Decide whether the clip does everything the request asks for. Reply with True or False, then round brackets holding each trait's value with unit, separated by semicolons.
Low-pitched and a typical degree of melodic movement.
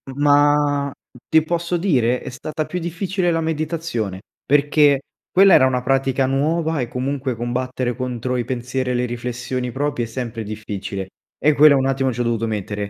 True (130 Hz; 3.6 semitones)